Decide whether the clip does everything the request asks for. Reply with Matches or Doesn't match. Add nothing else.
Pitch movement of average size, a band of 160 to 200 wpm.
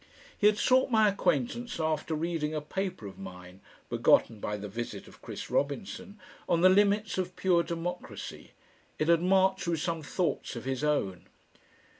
Doesn't match